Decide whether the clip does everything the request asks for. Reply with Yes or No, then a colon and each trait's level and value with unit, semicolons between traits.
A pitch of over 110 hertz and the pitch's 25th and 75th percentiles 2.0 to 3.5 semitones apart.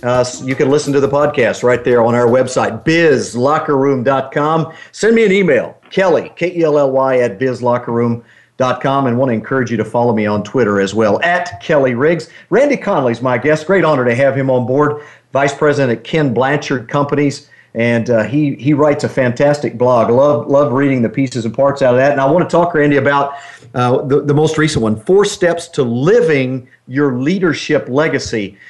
Yes: low, 135 Hz; average, 3.2 semitones